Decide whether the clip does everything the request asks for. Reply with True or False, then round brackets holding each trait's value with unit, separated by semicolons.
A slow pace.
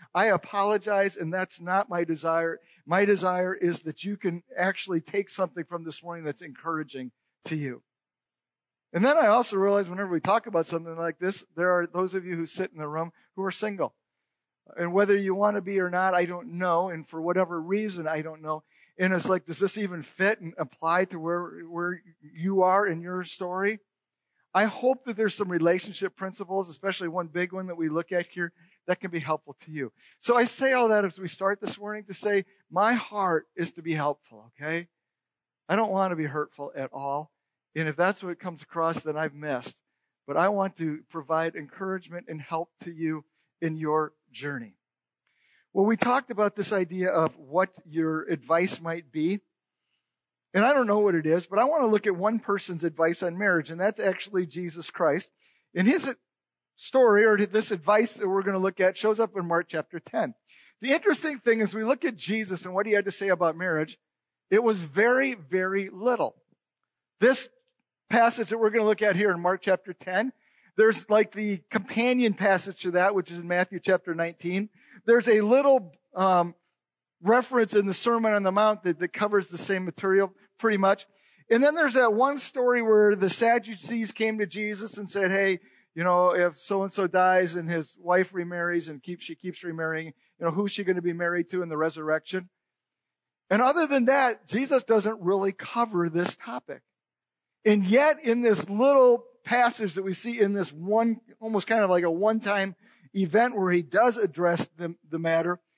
False (200 wpm)